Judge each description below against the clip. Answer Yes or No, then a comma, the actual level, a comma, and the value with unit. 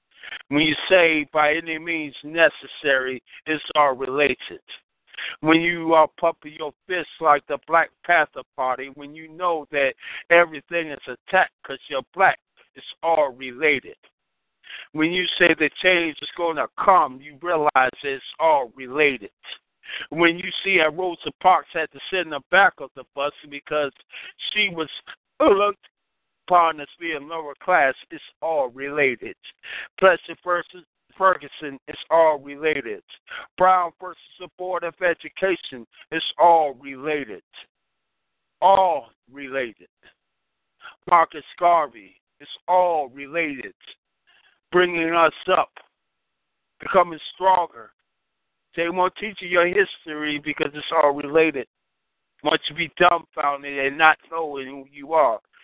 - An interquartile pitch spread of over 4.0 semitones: No, average, 3.3 semitones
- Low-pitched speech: No, medium, 160 Hz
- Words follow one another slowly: Yes, slow, 130 wpm